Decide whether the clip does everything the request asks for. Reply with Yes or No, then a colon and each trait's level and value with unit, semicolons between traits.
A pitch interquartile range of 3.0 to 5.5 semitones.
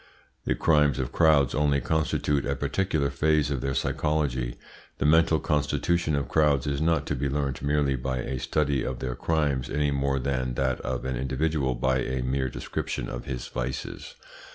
No: narrow, 2.4 semitones